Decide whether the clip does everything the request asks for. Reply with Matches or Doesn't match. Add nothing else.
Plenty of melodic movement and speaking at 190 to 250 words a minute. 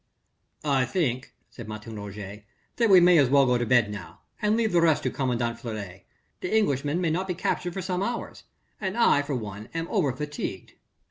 Matches